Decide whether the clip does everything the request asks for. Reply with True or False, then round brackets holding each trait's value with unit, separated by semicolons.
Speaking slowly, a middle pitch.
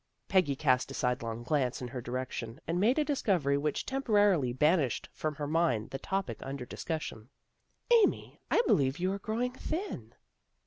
False (175 wpm; 150 Hz)